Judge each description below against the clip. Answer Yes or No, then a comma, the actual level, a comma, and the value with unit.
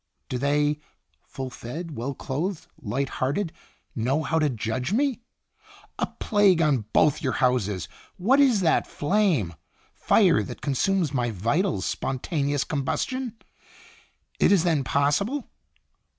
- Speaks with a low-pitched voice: No, medium, 145 Hz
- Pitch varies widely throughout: Yes, wide, 6.4 semitones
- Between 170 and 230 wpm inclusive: No, slow, 135 wpm